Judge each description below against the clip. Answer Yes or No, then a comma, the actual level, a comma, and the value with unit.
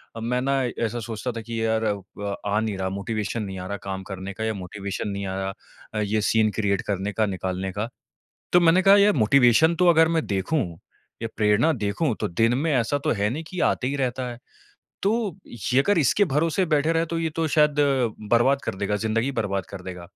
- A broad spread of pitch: Yes, wide, 6.6 semitones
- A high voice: No, low, 115 Hz